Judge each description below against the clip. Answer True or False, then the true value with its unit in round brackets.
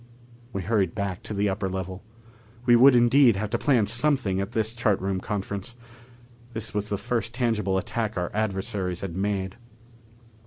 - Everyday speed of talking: True (165 wpm)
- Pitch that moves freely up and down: False (3.3 semitones)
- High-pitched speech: False (105 Hz)